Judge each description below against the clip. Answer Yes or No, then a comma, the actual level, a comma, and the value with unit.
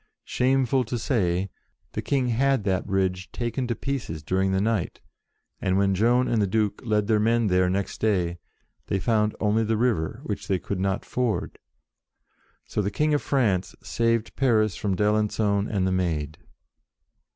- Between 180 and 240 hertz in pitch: No, low, 105 Hz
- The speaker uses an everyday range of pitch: Yes, average, 3.7 semitones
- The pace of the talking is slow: No, average, 165 wpm